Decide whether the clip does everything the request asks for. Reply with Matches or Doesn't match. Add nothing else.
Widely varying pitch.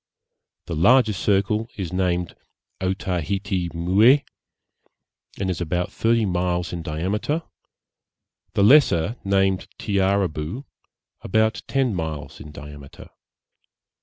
Doesn't match